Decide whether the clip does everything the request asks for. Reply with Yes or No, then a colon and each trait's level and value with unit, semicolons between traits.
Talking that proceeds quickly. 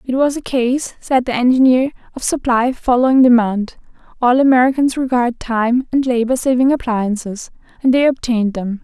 No: average, 150 wpm